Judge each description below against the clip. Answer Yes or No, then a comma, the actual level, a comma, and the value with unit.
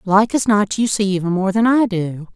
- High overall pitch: Yes, high, 200 Hz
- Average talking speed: No, fast, 255 wpm